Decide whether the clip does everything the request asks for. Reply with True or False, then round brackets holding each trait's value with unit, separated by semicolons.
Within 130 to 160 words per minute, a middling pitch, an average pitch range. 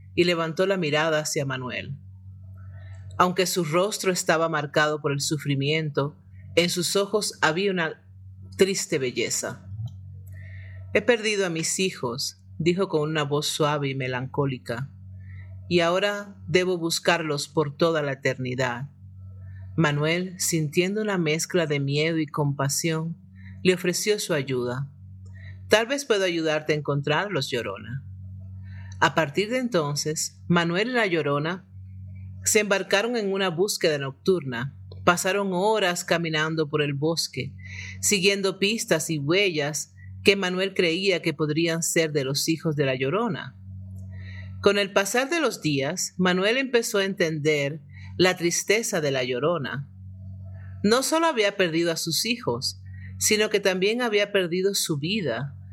False (135 wpm; 155 Hz; 7.5 semitones)